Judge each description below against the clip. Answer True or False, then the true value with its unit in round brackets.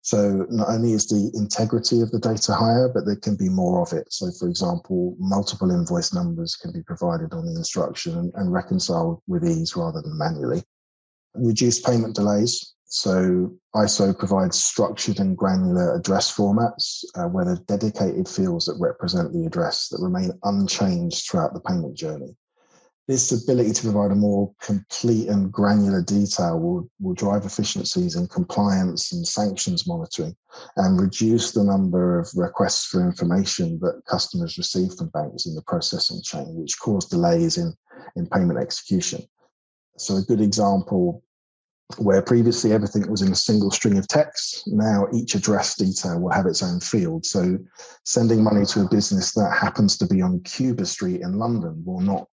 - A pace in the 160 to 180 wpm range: True (170 wpm)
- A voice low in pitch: False (160 Hz)